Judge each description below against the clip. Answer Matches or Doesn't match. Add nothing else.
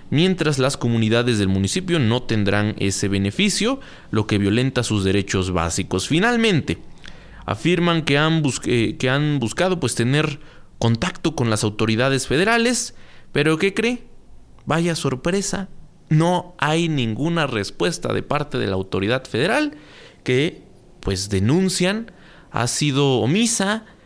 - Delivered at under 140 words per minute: Matches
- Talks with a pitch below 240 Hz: Matches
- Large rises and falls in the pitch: Matches